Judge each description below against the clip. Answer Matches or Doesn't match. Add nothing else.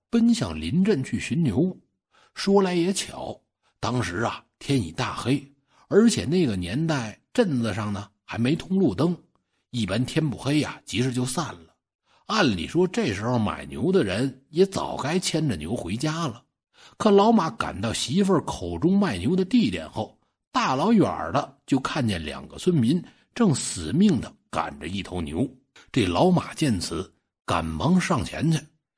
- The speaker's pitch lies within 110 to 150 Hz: Matches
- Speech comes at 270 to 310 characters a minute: Doesn't match